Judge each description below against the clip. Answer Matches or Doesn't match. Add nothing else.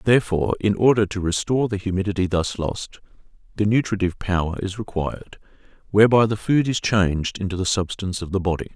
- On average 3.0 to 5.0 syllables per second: Doesn't match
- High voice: Doesn't match